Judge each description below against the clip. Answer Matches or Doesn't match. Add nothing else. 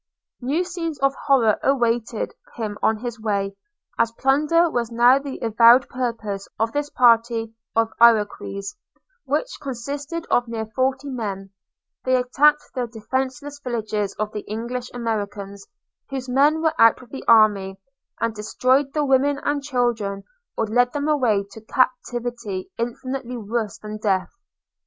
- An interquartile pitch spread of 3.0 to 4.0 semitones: Matches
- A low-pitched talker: Doesn't match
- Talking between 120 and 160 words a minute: Matches